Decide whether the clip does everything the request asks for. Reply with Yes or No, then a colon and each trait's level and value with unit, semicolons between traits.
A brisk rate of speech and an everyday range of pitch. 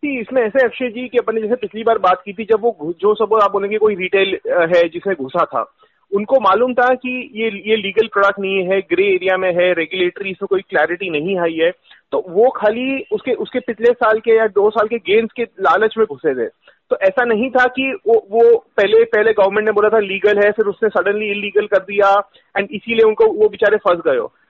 Yes: fast, 225 wpm; average, 4.1 semitones